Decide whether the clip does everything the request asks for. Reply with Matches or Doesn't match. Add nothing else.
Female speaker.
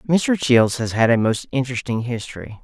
Doesn't match